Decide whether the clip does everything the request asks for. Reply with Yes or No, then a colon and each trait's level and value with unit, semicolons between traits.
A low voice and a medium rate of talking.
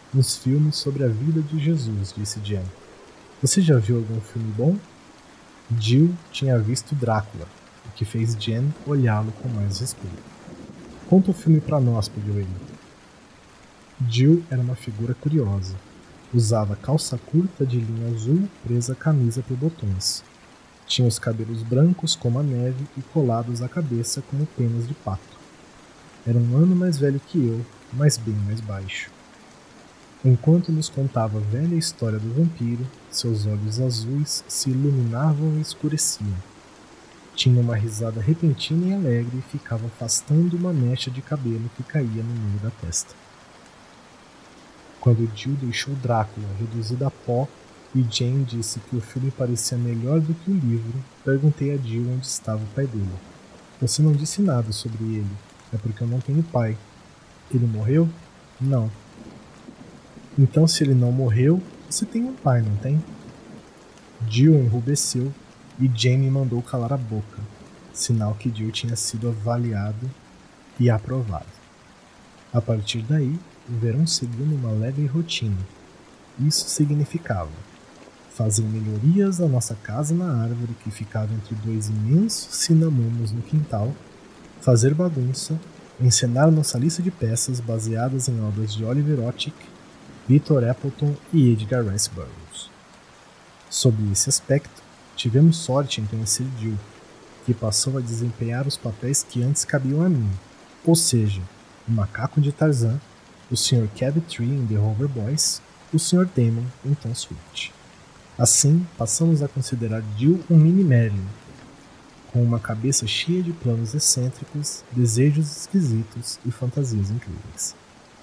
Yes: low, 125 Hz; average, 145 wpm